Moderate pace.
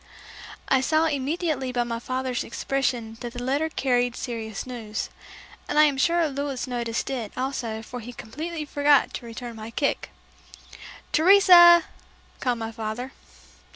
Yes: average, 145 wpm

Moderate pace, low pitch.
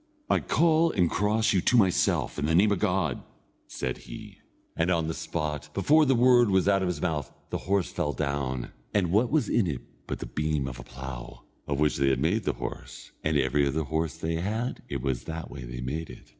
No: fast, 225 wpm; very low, 80 Hz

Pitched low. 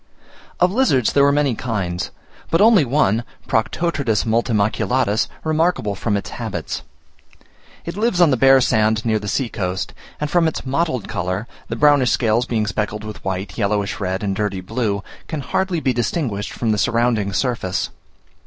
Yes: low, 115 Hz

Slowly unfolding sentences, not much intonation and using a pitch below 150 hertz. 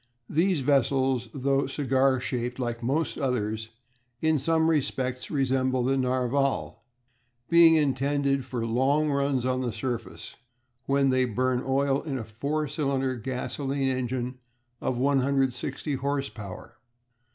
Yes: slow, 125 wpm; narrow, 1.8 semitones; low, 135 Hz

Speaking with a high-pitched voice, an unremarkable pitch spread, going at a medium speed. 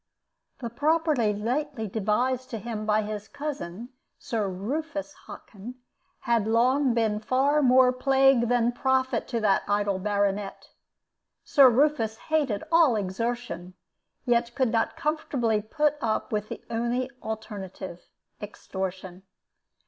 No: high, 235 Hz; average, 3.9 semitones; slow, 120 wpm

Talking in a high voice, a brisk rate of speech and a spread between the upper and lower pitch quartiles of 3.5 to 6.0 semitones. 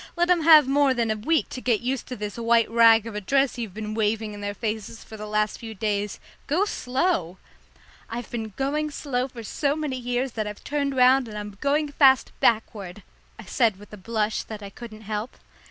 Yes: high, 230 Hz; fast, 220 wpm; average, 4.1 semitones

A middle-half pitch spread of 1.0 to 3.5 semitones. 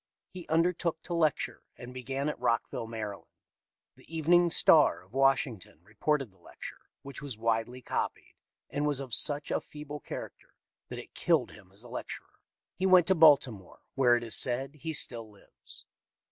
No: average, 4.9 semitones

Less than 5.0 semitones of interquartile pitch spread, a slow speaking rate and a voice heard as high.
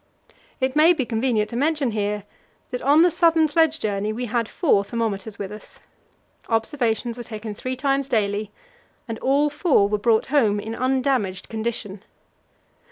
No: average, 4.6 semitones; average, 160 wpm; high, 235 Hz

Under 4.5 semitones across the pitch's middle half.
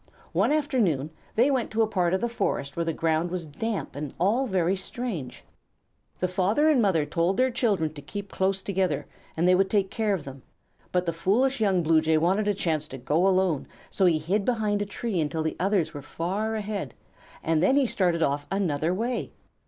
No: average, 4.8 semitones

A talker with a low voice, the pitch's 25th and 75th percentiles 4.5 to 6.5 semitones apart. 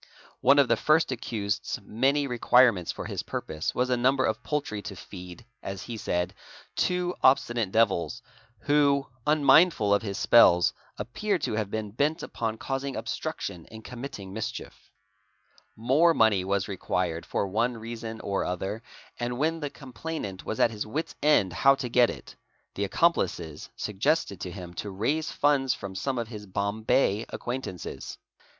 Yes: low, 115 Hz; wide, 5.5 semitones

